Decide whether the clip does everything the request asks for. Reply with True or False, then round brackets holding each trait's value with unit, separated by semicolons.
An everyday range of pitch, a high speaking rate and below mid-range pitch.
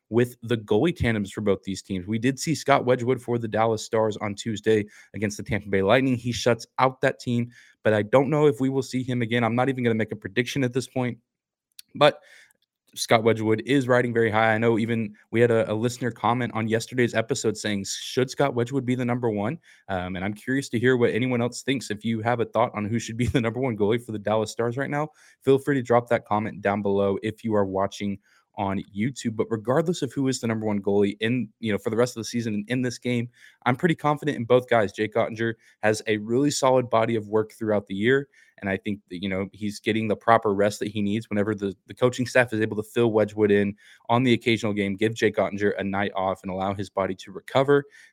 True (3.0 semitones; 250 wpm; 115 Hz)